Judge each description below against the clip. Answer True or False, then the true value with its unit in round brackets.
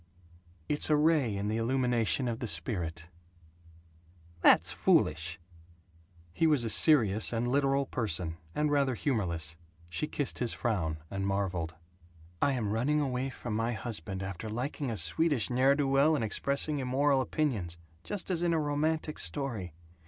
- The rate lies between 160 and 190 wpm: False (150 wpm)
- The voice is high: False (120 Hz)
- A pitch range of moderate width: False (6.5 semitones)